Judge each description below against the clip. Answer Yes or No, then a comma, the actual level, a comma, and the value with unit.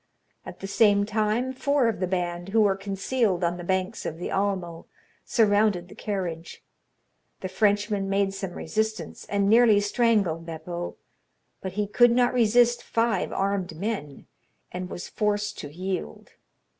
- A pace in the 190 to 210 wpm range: No, average, 150 wpm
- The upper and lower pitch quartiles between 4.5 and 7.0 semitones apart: No, average, 3.3 semitones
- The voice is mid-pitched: No, high, 200 Hz